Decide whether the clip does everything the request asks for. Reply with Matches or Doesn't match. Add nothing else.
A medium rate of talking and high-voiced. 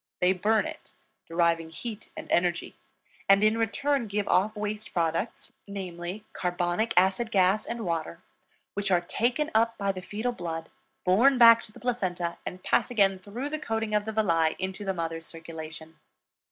Matches